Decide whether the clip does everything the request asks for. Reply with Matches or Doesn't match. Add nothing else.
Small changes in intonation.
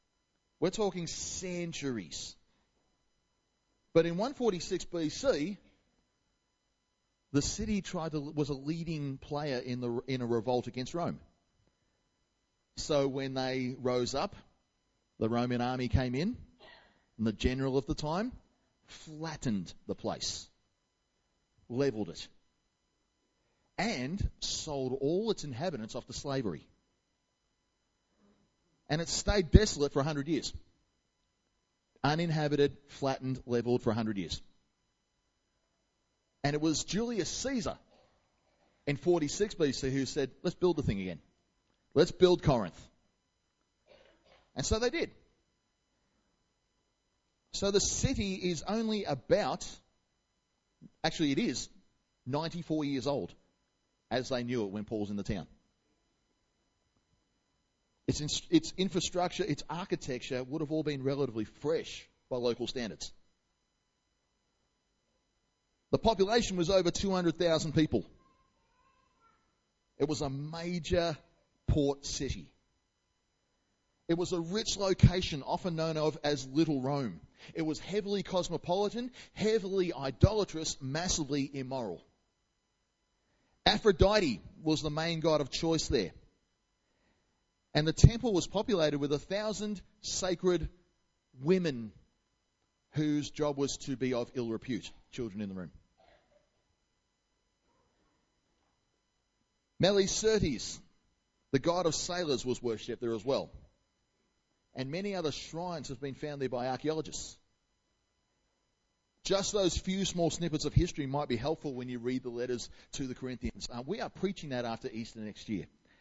Doesn't match